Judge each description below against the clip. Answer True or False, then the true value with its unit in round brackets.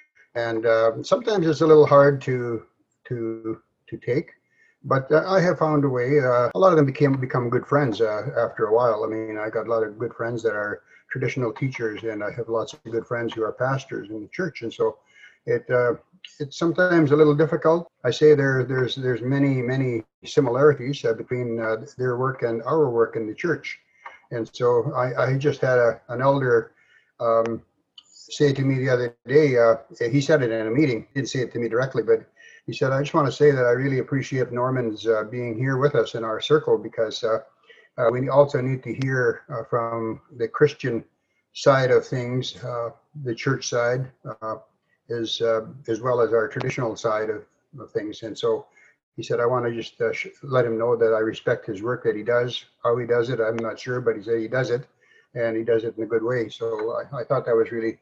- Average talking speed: False (220 wpm)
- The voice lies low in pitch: True (125 Hz)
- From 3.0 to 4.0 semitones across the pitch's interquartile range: False (4.4 semitones)